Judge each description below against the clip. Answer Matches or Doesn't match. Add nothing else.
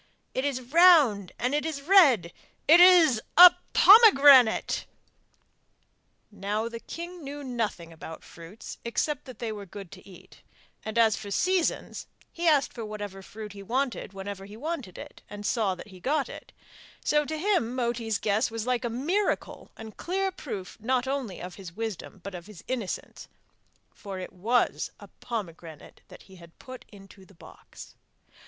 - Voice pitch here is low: Doesn't match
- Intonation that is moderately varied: Doesn't match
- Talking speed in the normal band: Matches